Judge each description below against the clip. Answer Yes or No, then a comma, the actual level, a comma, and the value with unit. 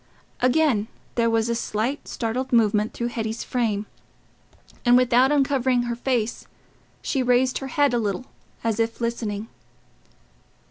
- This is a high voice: Yes, high, 235 Hz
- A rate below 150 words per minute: Yes, slow, 135 wpm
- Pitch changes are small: Yes, narrow, 2.3 semitones